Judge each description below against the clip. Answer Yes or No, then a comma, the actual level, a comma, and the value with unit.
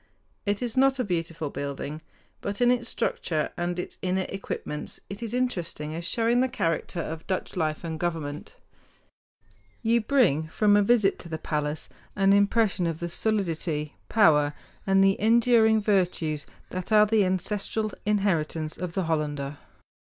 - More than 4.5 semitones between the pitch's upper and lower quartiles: Yes, average, 5.2 semitones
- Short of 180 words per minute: Yes, average, 155 wpm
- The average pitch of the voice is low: No, medium, 185 Hz